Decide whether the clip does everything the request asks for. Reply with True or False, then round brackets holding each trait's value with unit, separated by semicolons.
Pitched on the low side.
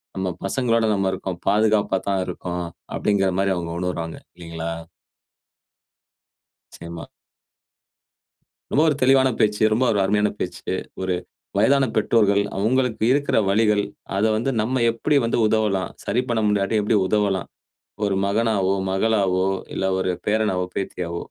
True (100 Hz)